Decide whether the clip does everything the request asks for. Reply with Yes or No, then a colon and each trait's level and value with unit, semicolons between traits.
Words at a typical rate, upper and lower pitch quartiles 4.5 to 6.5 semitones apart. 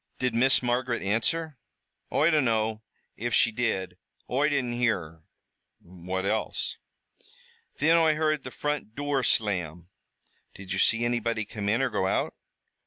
Yes: average, 145 wpm; average, 4.9 semitones